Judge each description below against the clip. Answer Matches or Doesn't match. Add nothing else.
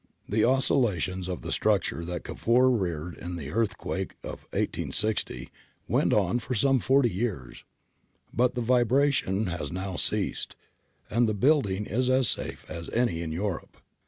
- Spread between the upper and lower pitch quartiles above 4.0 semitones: Matches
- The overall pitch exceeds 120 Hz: Doesn't match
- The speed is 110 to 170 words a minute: Matches